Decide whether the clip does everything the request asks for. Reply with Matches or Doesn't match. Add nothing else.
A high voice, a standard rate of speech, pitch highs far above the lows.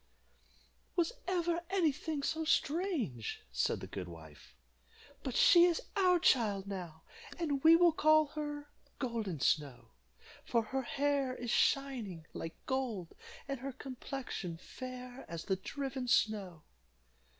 Doesn't match